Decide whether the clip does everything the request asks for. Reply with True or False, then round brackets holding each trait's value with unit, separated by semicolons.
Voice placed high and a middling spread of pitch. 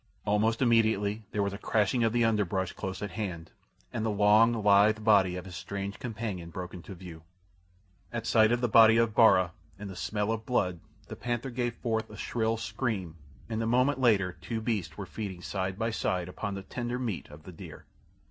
False (105 Hz; 3.2 semitones)